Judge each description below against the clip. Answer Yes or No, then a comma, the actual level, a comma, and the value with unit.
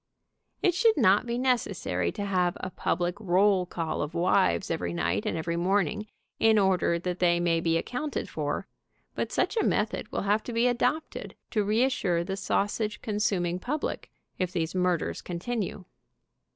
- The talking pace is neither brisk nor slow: Yes, average, 165 wpm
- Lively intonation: No, average, 4.1 semitones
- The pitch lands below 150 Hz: No, high, 190 Hz